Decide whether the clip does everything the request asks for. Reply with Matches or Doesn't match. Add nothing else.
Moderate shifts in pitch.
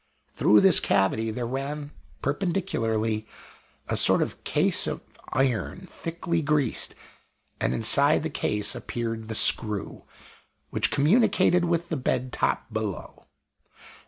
Doesn't match